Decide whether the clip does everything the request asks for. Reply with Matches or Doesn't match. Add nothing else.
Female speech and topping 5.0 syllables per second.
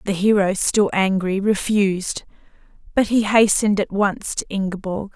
Doesn't match